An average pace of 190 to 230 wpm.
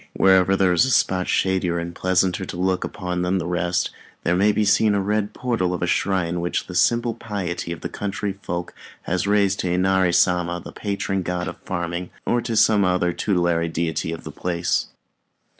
Yes: average, 195 wpm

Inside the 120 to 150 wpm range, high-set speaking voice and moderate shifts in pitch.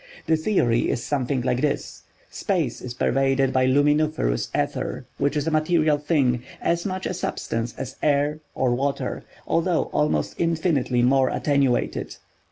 No: average, 140 wpm; medium, 140 Hz; average, 3.4 semitones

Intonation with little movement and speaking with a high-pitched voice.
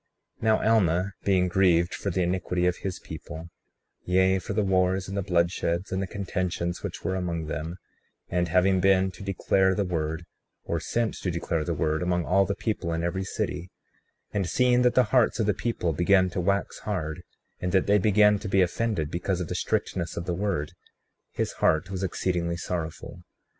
No: narrow, 2.3 semitones; very low, 90 Hz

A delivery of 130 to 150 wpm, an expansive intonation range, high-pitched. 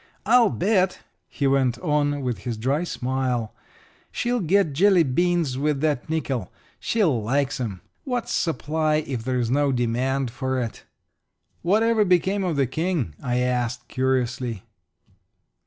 No: average, 140 wpm; wide, 5.8 semitones; medium, 140 Hz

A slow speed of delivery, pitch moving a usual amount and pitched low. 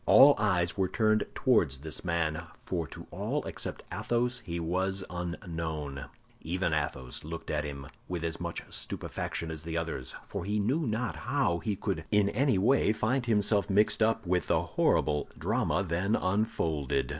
No: average, 160 wpm; average, 4.8 semitones; very low, 90 Hz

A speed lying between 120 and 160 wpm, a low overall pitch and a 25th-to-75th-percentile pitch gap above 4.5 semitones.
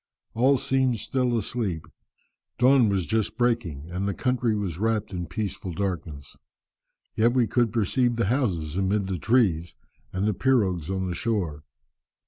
Yes: average, 155 wpm; low, 105 Hz; average, 5.0 semitones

